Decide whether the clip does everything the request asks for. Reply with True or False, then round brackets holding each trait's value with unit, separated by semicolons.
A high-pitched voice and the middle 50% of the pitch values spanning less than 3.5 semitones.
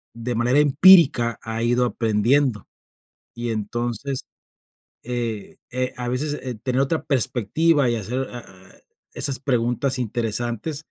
False (120 Hz; 2.6 semitones)